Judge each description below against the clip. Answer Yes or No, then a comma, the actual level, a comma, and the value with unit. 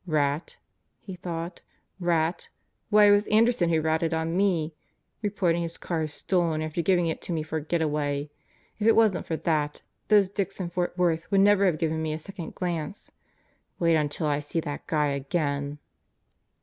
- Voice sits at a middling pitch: Yes, medium, 165 Hz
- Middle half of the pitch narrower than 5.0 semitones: Yes, average, 3.0 semitones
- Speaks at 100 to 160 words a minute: No, average, 185 wpm